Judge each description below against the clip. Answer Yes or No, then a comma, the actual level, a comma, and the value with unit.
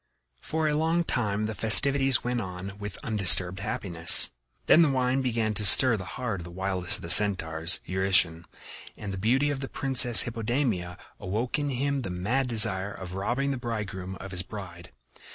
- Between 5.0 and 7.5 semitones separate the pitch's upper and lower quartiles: Yes, wide, 5.5 semitones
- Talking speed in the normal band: Yes, average, 180 wpm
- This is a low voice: Yes, low, 105 Hz